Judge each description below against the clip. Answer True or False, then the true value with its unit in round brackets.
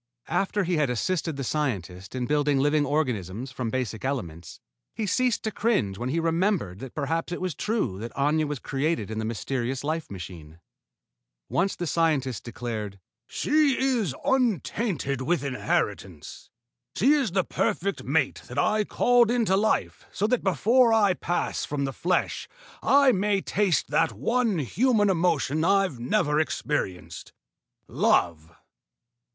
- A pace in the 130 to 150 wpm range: True (145 wpm)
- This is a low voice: False (155 Hz)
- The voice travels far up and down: True (8.2 semitones)